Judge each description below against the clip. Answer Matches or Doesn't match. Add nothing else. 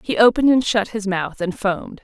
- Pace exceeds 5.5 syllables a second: Matches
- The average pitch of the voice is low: Doesn't match